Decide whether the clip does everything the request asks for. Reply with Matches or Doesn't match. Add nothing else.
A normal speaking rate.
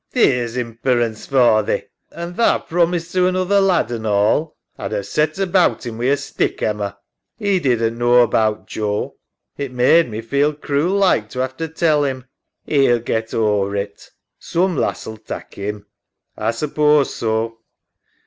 Matches